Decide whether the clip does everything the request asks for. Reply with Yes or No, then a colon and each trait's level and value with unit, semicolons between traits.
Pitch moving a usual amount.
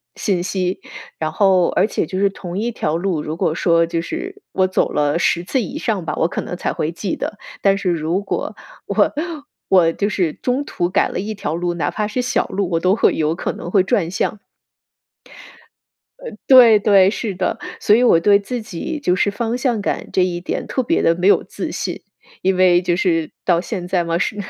Yes: average, 3.5 semitones